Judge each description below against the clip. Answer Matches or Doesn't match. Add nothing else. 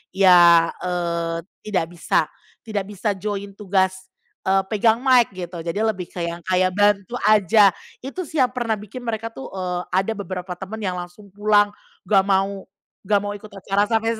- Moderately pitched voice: Doesn't match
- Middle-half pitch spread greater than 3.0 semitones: Doesn't match